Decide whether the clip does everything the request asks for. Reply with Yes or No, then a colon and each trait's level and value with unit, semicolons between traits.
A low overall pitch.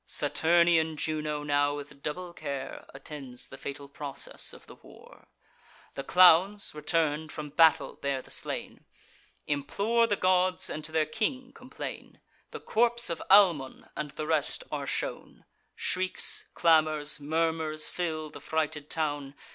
No: medium, 155 Hz